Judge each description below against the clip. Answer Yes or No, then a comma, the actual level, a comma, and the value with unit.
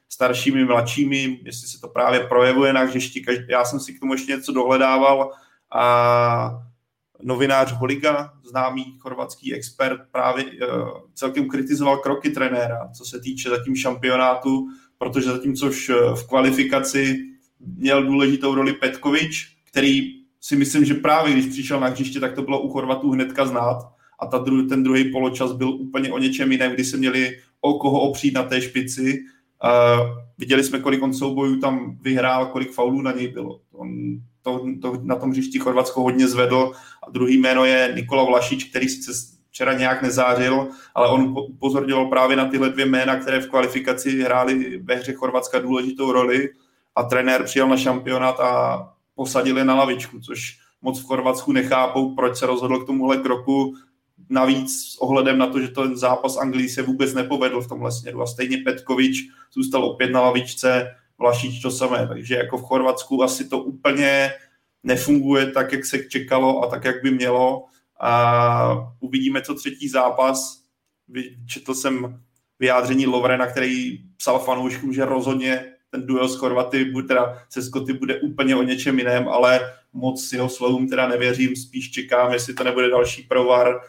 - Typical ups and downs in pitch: No, narrow, 1.1 semitones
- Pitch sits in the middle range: No, low, 130 Hz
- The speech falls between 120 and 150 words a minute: No, average, 165 wpm